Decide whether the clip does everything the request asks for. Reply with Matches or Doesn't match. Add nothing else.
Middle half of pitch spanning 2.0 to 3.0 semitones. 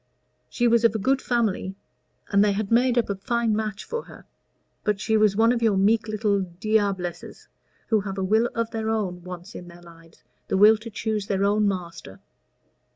Matches